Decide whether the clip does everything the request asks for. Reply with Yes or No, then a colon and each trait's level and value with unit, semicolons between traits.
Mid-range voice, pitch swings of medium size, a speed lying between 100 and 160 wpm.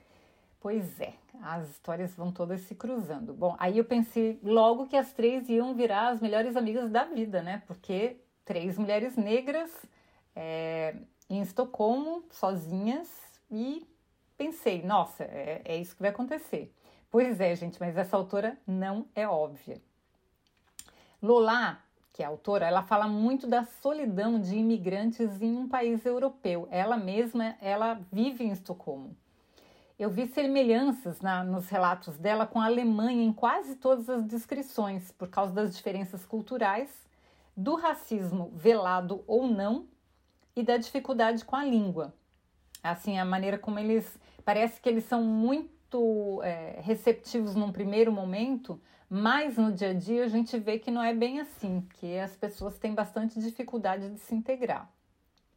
No: high, 220 Hz; average, 4.0 semitones; average, 150 wpm